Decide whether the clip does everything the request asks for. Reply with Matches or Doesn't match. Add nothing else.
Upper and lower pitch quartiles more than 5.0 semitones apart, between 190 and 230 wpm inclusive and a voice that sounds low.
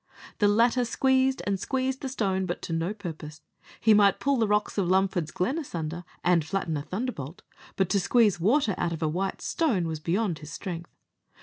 Doesn't match